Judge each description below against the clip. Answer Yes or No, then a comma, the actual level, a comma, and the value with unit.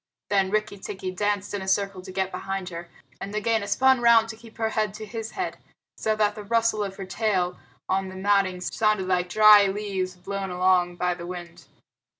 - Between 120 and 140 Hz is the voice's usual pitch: No, high, 195 Hz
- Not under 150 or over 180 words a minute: No, average, 200 wpm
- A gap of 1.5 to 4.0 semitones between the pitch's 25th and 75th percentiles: Yes, narrow, 2.4 semitones